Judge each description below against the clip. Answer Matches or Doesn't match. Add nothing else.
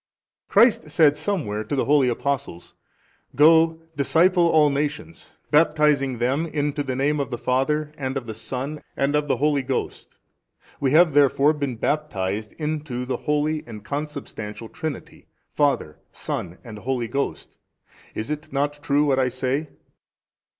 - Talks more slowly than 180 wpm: Matches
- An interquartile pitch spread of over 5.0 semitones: Doesn't match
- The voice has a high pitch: Doesn't match